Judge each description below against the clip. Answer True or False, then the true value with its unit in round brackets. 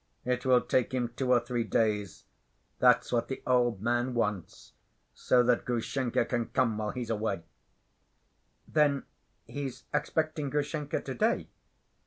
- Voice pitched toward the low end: True (125 Hz)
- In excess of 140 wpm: False (135 wpm)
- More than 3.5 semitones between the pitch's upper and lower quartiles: False (2.4 semitones)